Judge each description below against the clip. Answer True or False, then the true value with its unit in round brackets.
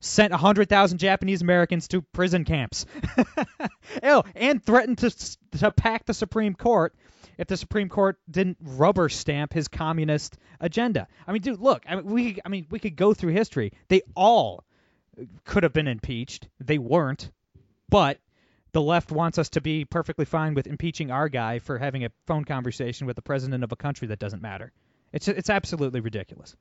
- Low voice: False (165 Hz)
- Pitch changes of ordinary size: False (6.3 semitones)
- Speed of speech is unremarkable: True (180 wpm)